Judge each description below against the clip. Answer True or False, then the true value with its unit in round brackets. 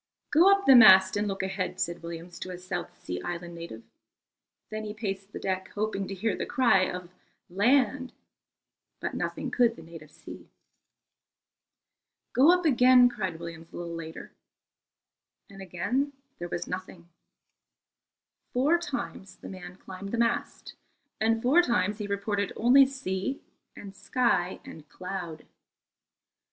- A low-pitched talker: False (195 Hz)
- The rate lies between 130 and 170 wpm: True (145 wpm)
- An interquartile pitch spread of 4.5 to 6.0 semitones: True (5.3 semitones)